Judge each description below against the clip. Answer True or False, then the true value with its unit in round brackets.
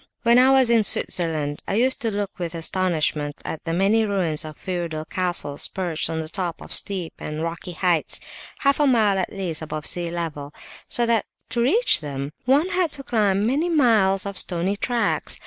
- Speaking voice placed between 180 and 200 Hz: True (190 Hz)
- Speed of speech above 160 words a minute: True (190 wpm)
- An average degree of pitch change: False (6.1 semitones)